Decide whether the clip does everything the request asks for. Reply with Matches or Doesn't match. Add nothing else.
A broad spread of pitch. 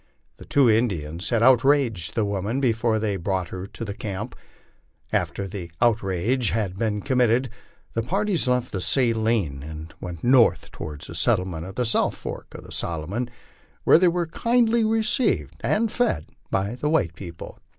Matches